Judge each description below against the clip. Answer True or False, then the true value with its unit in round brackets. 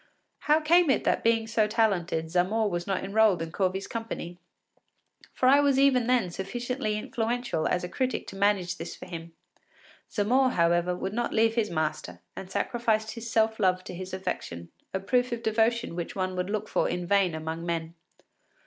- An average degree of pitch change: True (4.6 semitones)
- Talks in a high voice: True (205 Hz)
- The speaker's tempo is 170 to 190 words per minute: True (185 wpm)